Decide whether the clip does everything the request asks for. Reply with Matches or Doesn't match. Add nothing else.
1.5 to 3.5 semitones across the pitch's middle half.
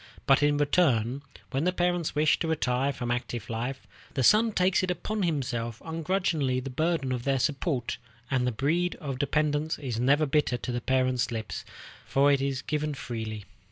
Doesn't match